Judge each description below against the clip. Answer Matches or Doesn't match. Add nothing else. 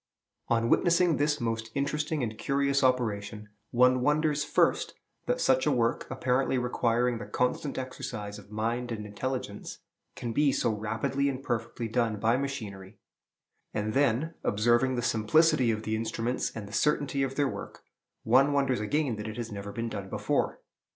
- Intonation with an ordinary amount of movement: Matches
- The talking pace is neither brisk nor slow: Matches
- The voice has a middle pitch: Doesn't match